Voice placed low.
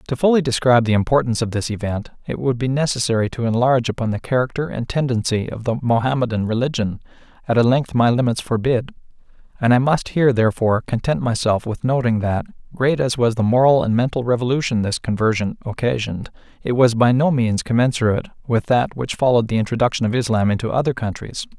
Yes: low, 120 Hz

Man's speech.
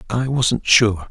Yes: male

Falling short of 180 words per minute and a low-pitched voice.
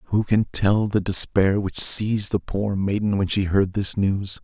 No: fast, 205 wpm; low, 100 Hz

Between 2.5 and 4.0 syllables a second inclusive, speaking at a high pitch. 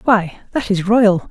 Yes: 3.7 syllables/s; high, 205 Hz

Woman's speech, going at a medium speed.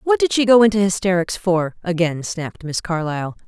Yes: female; average, 190 wpm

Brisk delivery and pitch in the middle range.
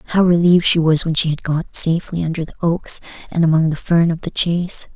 Yes: fast, 230 wpm; medium, 165 Hz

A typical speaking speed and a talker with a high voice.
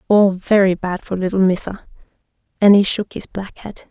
Yes: average, 185 wpm; high, 195 Hz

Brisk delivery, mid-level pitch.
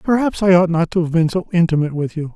Yes: fast, 280 wpm; medium, 170 Hz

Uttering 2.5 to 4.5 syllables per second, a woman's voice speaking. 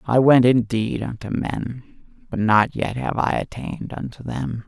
No: 4.3 syllables/s; male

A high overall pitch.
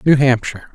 No: low, 130 Hz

